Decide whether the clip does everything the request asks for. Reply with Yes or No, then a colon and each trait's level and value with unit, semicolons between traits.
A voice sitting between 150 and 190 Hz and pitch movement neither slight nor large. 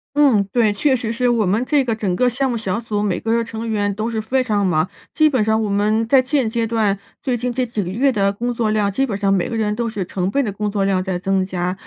No: high, 220 Hz; average, 3.3 semitones